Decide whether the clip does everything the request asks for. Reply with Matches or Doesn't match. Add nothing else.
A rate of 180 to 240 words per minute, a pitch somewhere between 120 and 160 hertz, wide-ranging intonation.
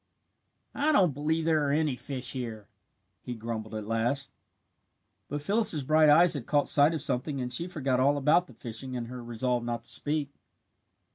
Doesn't match